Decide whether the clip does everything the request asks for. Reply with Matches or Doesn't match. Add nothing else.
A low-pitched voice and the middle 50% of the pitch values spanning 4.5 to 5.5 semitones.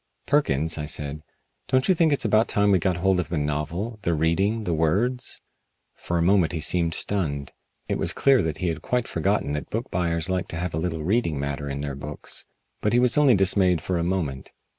Matches